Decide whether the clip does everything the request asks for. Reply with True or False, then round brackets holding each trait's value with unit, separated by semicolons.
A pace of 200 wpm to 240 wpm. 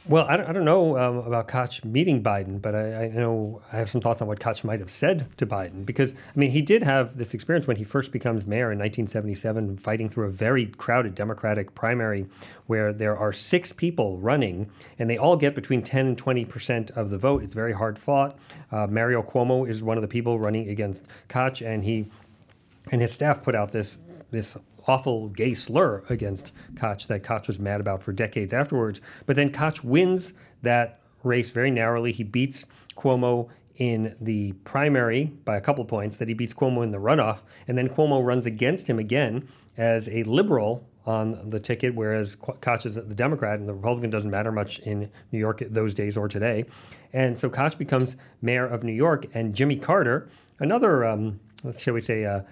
True (205 wpm)